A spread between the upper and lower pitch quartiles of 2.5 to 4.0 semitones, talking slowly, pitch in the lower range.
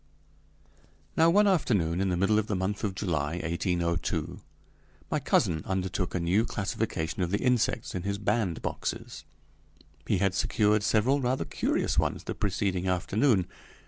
No: average, 3.4 semitones; average, 145 wpm; low, 100 Hz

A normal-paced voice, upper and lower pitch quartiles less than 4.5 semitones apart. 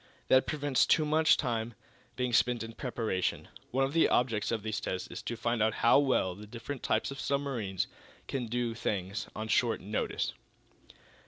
Yes: average, 175 wpm; average, 3.5 semitones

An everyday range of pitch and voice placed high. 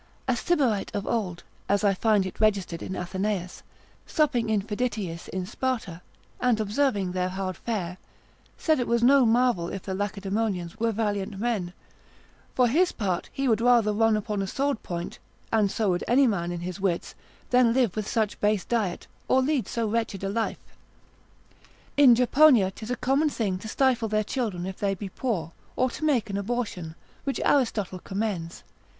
Yes: average, 4.2 semitones; high, 215 Hz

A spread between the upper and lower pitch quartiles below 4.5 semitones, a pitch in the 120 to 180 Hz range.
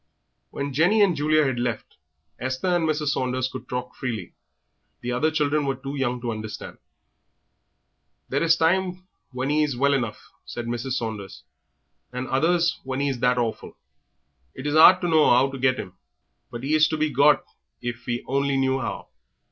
Yes: average, 3.7 semitones; low, 135 Hz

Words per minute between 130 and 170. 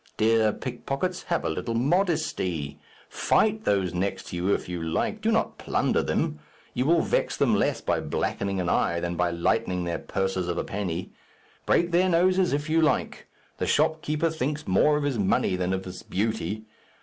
No: average, 185 wpm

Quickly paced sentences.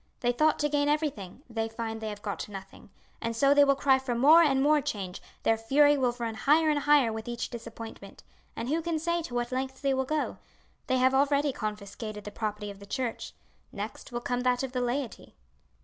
Yes: fast, 215 wpm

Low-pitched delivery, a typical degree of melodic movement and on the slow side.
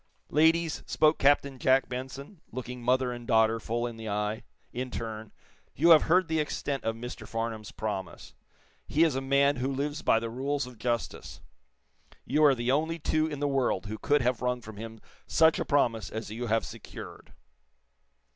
No: low, 125 Hz; average, 4.2 semitones; average, 185 wpm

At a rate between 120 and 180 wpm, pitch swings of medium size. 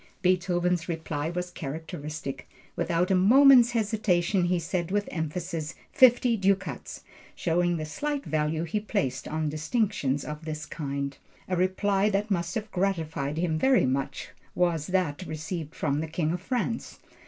Yes: average, 145 wpm; average, 4.0 semitones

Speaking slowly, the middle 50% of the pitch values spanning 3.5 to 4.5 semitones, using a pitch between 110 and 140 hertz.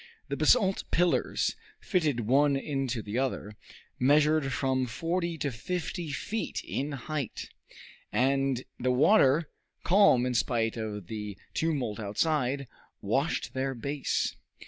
Yes: slow, 120 wpm; average, 3.9 semitones; low, 135 Hz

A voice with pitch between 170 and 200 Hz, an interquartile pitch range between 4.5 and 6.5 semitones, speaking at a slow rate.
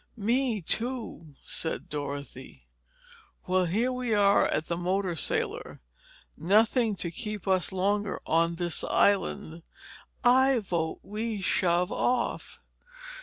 Yes: high, 190 Hz; average, 4.9 semitones; slow, 115 wpm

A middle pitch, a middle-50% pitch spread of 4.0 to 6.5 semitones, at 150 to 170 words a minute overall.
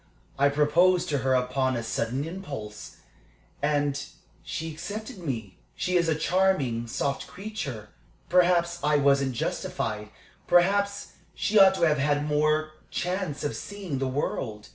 No: medium, 150 Hz; average, 5.1 semitones; average, 140 wpm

